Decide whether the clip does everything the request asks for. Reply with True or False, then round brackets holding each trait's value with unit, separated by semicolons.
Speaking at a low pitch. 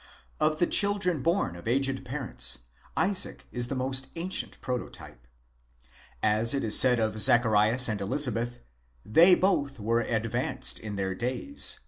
True (125 Hz)